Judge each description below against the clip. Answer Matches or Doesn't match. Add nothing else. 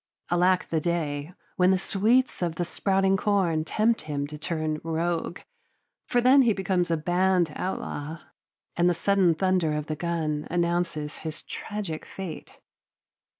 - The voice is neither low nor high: Matches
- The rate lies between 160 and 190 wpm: Doesn't match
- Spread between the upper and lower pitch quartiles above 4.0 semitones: Doesn't match